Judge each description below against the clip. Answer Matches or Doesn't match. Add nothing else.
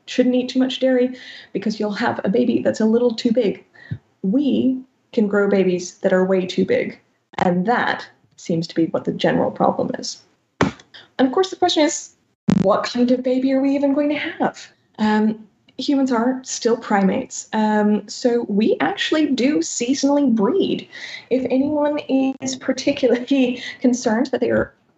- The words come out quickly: Doesn't match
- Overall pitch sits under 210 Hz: Doesn't match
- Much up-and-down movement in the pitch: Doesn't match